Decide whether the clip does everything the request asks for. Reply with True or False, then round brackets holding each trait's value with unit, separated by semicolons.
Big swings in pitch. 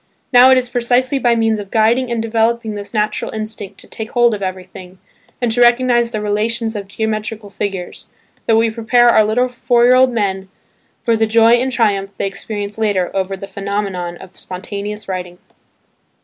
False (3.0 semitones)